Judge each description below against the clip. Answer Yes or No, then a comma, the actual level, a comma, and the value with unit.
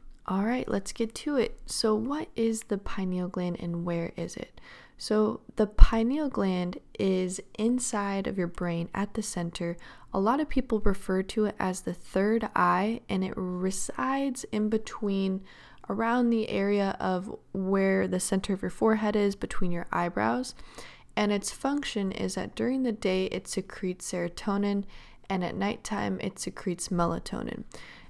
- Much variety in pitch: No, average, 3.2 semitones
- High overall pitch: Yes, high, 200 Hz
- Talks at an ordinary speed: Yes, average, 160 wpm